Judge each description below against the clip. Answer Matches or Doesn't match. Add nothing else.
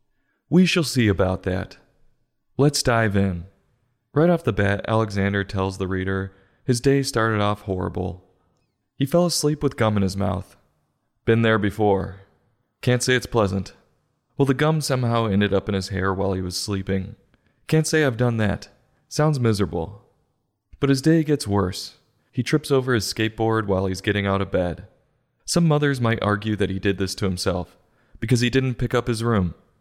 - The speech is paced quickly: Doesn't match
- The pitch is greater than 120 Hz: Doesn't match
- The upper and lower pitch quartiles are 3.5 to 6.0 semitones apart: Matches